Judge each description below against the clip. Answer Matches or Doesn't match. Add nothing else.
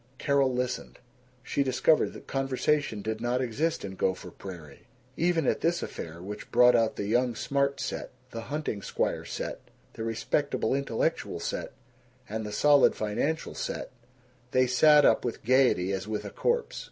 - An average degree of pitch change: Matches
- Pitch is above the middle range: Doesn't match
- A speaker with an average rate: Matches